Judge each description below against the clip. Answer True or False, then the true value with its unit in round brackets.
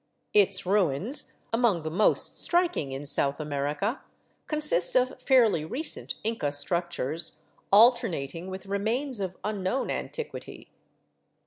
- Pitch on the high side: True (195 Hz)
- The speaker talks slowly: True (115 wpm)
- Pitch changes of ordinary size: False (7.2 semitones)